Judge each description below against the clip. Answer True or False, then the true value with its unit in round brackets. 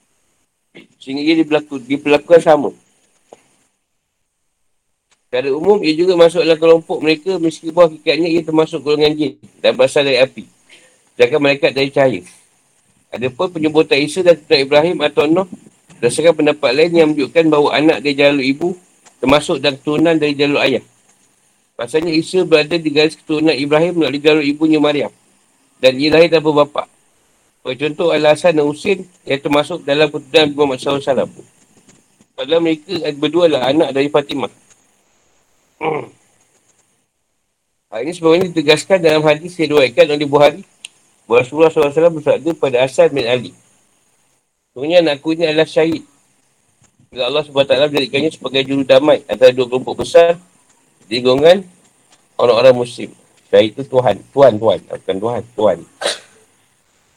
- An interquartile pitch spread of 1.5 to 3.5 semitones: True (3.0 semitones)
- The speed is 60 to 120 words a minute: False (145 wpm)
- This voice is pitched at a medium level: True (155 Hz)